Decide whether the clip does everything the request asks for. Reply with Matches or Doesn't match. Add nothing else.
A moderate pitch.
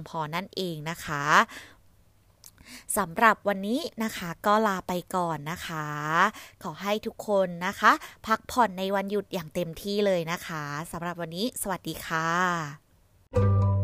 Matches